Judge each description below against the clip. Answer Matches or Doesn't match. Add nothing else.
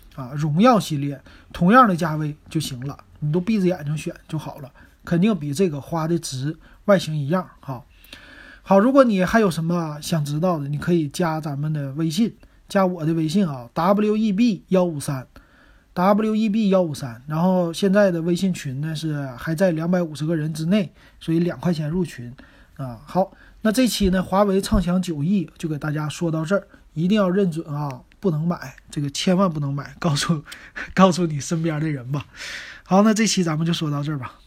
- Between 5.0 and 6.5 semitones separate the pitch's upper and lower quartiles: Doesn't match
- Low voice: Doesn't match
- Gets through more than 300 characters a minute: Doesn't match